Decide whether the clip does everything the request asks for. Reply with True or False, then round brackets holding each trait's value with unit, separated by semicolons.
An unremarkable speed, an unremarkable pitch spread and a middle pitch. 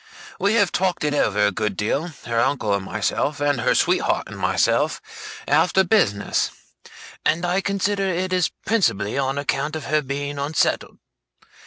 False (160 wpm; 7.0 semitones; 145 Hz)